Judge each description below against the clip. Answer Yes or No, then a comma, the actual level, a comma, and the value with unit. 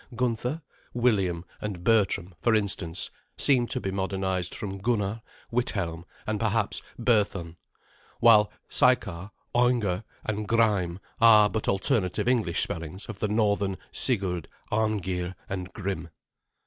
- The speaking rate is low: Yes, slow, 120 wpm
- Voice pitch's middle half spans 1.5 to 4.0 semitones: Yes, average, 3.5 semitones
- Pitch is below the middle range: Yes, low, 100 Hz